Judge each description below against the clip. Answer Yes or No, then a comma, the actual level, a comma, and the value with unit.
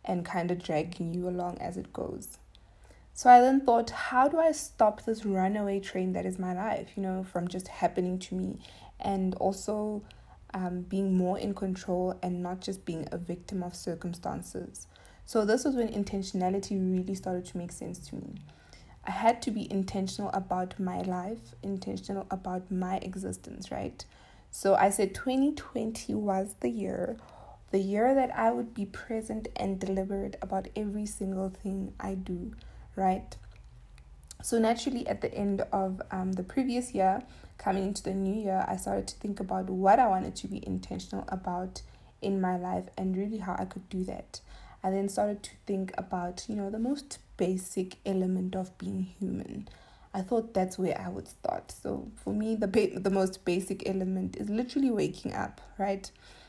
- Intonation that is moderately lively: No, narrow, 2.1 semitones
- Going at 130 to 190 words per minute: Yes, average, 175 wpm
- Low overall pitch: No, high, 195 Hz